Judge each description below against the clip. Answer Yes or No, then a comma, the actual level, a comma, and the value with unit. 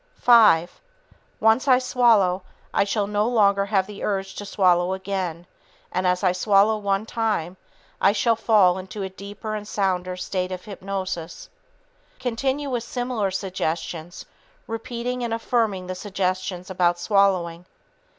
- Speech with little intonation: No, average, 3.3 semitones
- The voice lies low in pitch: No, high, 195 Hz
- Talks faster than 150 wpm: No, average, 140 wpm